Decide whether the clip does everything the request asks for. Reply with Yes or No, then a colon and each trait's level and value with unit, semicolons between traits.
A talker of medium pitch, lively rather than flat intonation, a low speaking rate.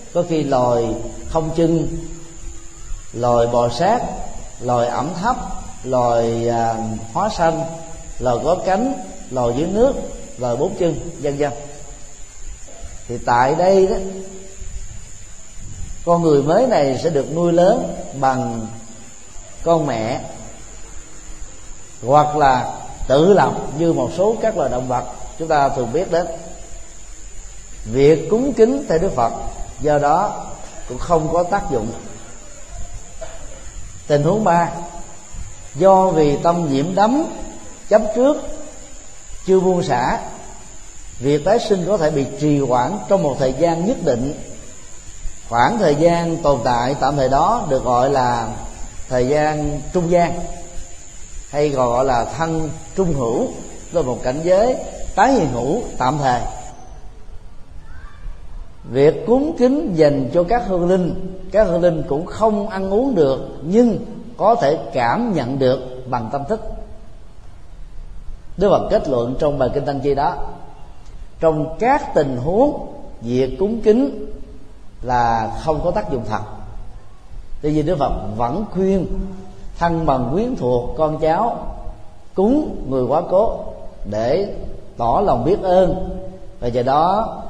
Yes: medium, 145 Hz; wide, 7.4 semitones; slow, 135 wpm